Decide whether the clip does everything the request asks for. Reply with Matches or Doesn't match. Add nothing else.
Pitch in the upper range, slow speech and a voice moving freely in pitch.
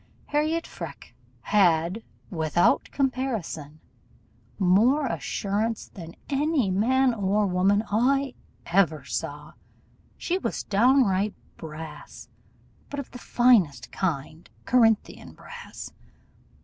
Matches